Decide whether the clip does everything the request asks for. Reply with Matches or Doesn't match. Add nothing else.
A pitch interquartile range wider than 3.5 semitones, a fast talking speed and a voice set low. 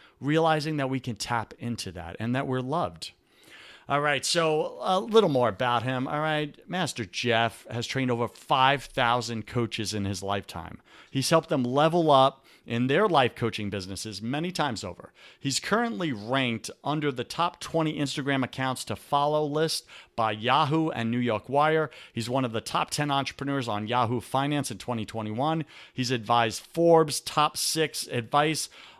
Doesn't match